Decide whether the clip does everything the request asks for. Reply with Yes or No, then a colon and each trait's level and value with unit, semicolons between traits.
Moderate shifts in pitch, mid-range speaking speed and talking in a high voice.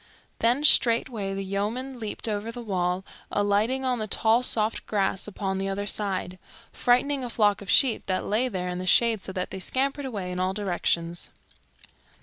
Yes: average, 3.8 semitones; average, 180 wpm; high, 205 Hz